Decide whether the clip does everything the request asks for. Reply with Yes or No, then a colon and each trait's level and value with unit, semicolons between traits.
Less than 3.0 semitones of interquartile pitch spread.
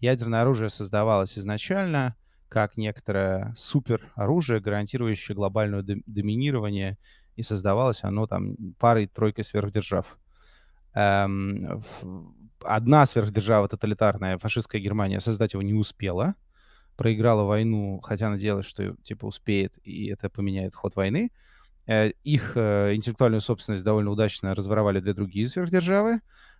Yes: narrow, 2.4 semitones